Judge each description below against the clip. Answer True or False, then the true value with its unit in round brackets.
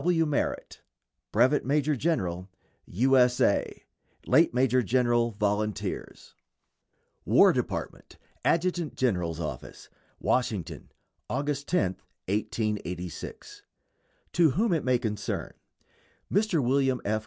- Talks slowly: True (100 wpm)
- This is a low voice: True (125 Hz)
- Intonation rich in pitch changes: True (5.9 semitones)